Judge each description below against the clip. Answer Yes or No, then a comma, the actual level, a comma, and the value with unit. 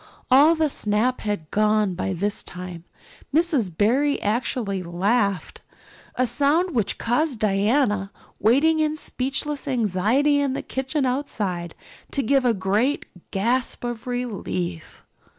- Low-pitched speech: No, high, 235 Hz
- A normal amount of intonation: No, wide, 5.8 semitones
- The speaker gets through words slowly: Yes, slow, 125 wpm